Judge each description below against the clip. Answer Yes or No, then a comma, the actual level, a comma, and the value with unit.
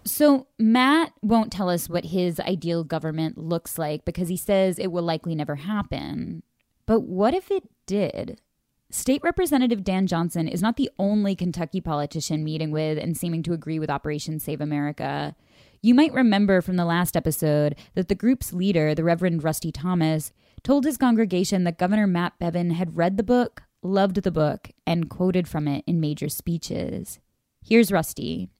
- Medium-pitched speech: Yes, medium, 175 Hz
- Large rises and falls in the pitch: No, average, 4.4 semitones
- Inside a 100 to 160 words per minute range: No, average, 170 wpm